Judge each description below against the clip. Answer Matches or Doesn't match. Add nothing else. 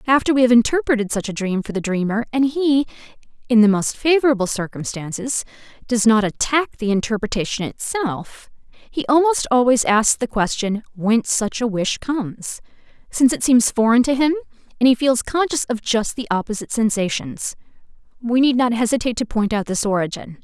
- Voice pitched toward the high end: Matches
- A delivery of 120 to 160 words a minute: Doesn't match